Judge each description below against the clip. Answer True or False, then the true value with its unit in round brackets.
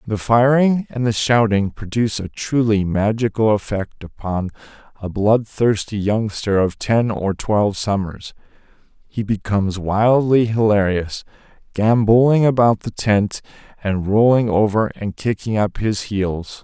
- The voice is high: False (110 Hz)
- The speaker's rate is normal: False (130 wpm)